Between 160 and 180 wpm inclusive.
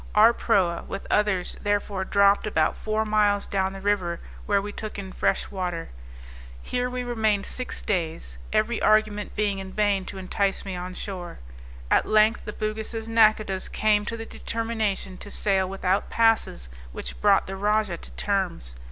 Yes: average, 165 wpm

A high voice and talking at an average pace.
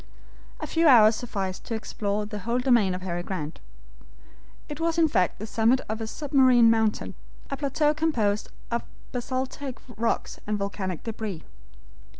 Yes: high, 225 Hz; average, 155 wpm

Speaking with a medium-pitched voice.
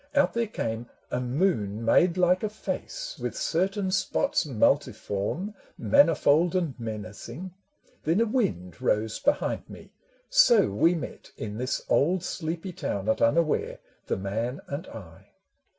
Yes: medium, 160 Hz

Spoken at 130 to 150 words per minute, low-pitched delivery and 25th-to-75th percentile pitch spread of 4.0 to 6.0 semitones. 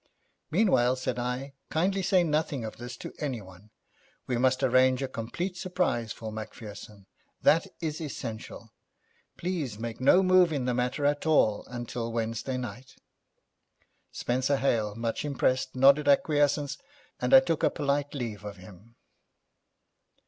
Yes: average, 140 wpm; low, 130 Hz; average, 4.4 semitones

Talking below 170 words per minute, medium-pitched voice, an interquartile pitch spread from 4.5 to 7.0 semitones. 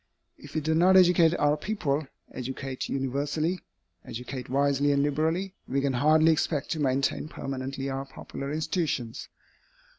No: average, 140 wpm; medium, 145 Hz; average, 2.8 semitones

